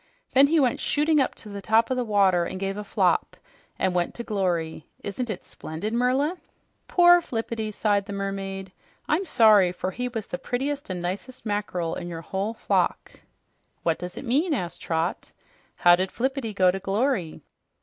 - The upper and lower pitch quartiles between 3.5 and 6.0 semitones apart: Yes, average, 5.3 semitones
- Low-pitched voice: No, high, 205 Hz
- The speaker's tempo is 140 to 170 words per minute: No, average, 180 wpm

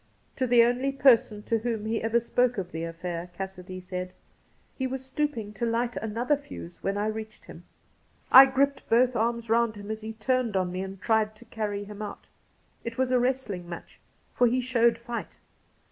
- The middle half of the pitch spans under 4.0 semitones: Yes, average, 3.3 semitones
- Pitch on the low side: No, high, 225 Hz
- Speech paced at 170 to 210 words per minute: Yes, average, 195 wpm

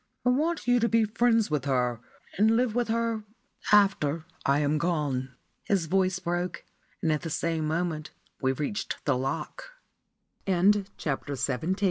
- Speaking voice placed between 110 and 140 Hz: No, medium, 175 Hz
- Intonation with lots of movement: Yes, wide, 6.7 semitones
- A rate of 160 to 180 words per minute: No, average, 150 wpm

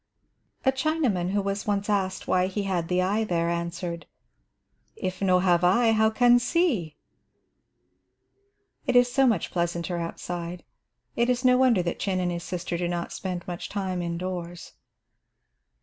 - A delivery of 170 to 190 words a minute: No, average, 155 wpm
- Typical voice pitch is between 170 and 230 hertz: Yes, medium, 185 Hz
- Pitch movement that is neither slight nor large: Yes, average, 4.0 semitones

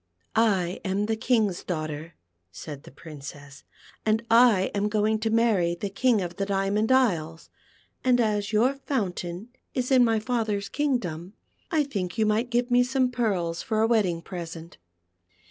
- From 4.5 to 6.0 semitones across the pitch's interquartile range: Yes, average, 5.1 semitones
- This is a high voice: Yes, high, 210 Hz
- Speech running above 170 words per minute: No, average, 165 wpm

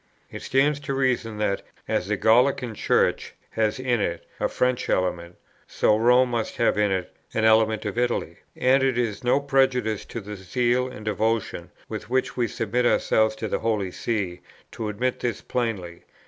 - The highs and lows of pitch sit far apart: No, average, 3.1 semitones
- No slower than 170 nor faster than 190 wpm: Yes, average, 175 wpm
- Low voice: Yes, low, 115 Hz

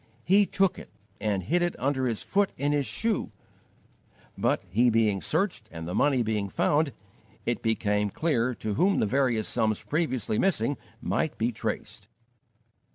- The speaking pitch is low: Yes, low, 125 Hz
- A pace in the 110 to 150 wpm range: No, average, 160 wpm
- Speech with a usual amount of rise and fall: No, wide, 6.5 semitones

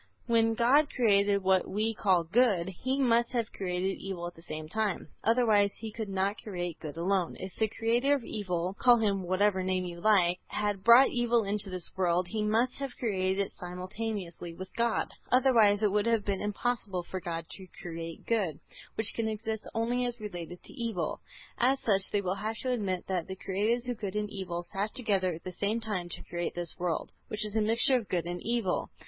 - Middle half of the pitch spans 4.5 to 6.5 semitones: No, average, 3.8 semitones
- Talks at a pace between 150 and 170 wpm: No, fast, 205 wpm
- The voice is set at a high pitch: Yes, high, 205 Hz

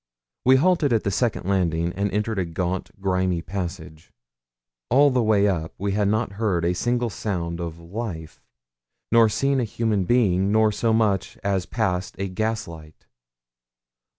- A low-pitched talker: Yes, low, 100 Hz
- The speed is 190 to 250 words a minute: No, average, 155 wpm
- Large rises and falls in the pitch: No, average, 4.0 semitones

